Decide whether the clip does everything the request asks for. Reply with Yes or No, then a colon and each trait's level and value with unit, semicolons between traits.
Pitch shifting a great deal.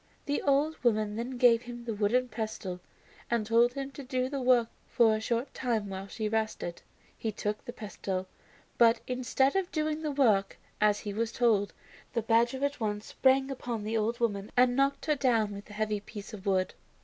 No: average, 3.3 semitones